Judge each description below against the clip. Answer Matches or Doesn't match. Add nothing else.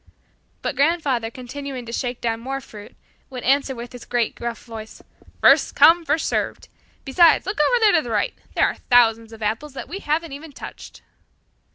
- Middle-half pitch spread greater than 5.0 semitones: Doesn't match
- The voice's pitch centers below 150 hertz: Doesn't match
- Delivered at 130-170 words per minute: Doesn't match